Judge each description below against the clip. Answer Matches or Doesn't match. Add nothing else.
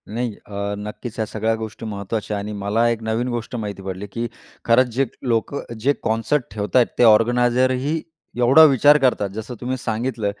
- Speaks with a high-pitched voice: Doesn't match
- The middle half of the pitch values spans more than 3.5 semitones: Doesn't match